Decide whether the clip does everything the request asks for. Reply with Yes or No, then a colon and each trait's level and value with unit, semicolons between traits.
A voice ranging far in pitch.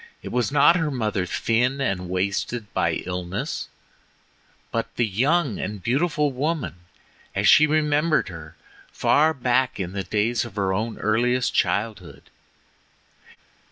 Yes: wide, 6.2 semitones